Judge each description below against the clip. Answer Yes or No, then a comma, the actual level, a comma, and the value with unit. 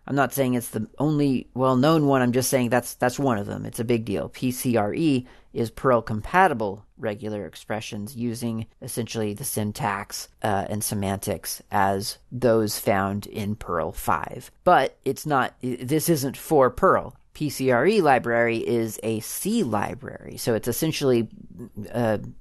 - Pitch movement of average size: Yes, average, 3.4 semitones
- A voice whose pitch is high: No, low, 115 Hz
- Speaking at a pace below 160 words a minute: Yes, average, 145 wpm